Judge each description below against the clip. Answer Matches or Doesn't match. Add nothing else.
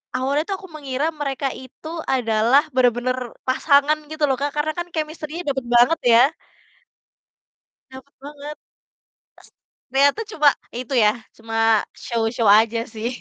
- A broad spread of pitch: Doesn't match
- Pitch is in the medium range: Doesn't match